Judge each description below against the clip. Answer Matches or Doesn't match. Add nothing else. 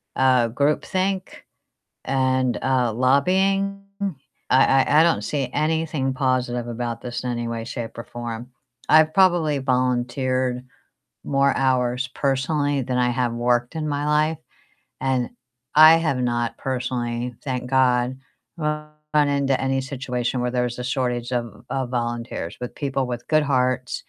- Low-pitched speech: Matches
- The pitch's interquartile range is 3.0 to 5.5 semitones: Doesn't match